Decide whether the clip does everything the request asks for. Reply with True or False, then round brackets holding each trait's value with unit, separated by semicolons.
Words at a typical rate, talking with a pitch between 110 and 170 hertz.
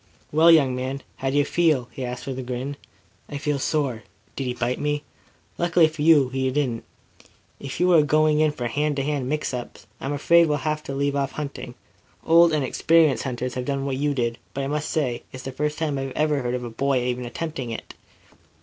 False (225 wpm; 140 Hz)